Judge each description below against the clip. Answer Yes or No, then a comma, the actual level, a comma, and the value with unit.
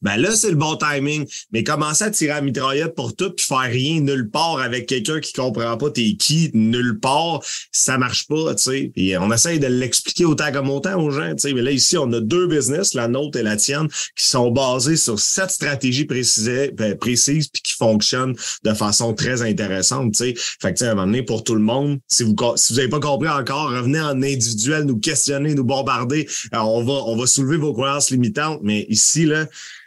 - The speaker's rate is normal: No, fast, 225 wpm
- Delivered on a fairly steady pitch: No, average, 4.2 semitones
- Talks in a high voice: No, low, 135 Hz